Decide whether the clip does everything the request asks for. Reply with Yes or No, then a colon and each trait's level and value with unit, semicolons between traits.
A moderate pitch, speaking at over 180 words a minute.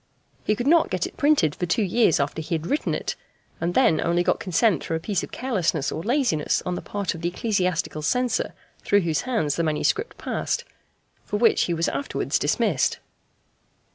Yes: medium, 180 Hz; average, 195 wpm